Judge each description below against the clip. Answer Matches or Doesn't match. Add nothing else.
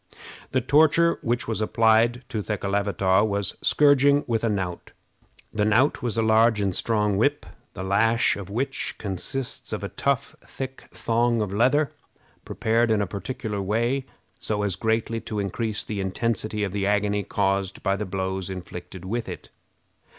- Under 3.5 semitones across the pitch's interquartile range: Matches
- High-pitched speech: Doesn't match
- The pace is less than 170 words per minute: Matches